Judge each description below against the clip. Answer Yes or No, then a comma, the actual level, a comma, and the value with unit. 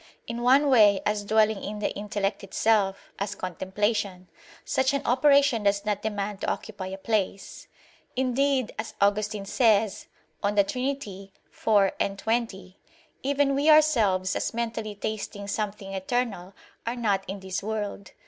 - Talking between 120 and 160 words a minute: Yes, average, 140 wpm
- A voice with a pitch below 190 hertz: No, high, 210 Hz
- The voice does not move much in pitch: No, average, 3.1 semitones